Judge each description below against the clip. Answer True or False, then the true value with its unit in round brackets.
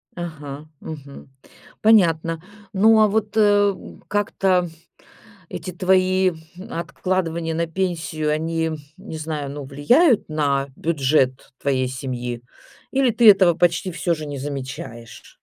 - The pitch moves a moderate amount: True (4.6 semitones)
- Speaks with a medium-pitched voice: True (165 Hz)